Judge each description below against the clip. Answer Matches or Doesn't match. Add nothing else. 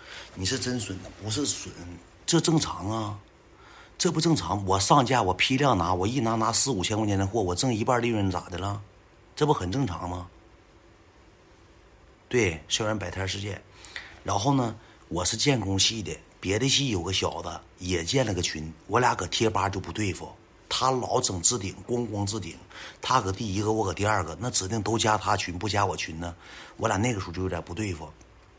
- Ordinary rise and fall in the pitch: Matches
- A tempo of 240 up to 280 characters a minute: Matches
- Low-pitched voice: Matches